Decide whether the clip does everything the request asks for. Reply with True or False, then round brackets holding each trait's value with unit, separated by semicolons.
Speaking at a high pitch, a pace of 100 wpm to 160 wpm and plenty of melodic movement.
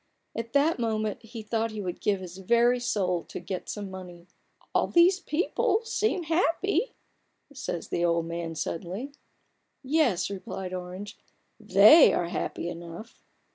True (210 Hz; 145 wpm; 6.0 semitones)